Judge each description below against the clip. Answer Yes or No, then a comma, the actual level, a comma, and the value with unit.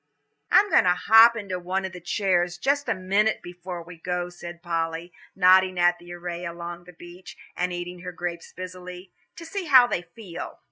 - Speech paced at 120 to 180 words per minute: No, average, 190 wpm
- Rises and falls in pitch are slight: Yes, narrow, 1.3 semitones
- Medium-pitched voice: Yes, medium, 180 Hz